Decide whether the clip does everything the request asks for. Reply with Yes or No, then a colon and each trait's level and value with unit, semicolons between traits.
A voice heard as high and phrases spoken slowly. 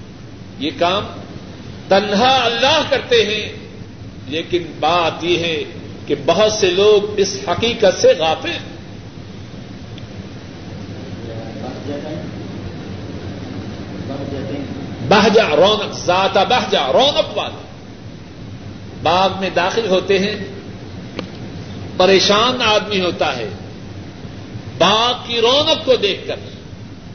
No: medium, 145 Hz; slow, 85 wpm